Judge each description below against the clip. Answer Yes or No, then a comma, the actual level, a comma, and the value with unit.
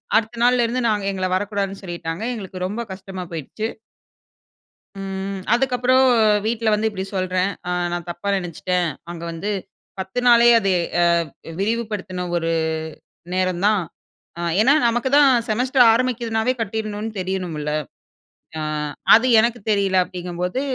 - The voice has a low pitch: No, high, 200 Hz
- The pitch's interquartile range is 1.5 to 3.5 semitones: No, average, 4.1 semitones